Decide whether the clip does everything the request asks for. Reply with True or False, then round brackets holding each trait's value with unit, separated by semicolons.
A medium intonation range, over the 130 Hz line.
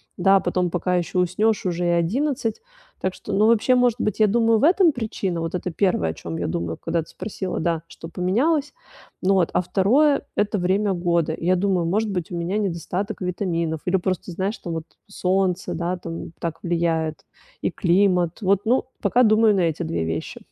True (3.7 semitones; 185 Hz)